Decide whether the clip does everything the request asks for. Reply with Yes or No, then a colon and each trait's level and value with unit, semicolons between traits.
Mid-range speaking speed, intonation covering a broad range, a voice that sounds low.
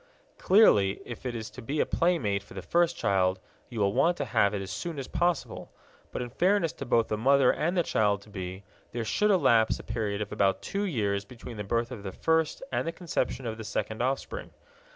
No: fast, 225 wpm; wide, 8.0 semitones; low, 120 Hz